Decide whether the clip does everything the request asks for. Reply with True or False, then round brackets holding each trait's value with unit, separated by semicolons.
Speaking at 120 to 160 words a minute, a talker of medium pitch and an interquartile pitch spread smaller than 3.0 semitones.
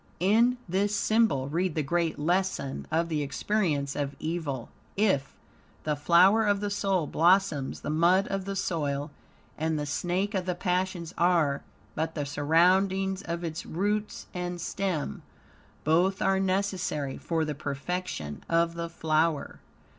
False (145 wpm; 170 Hz; 4.0 semitones)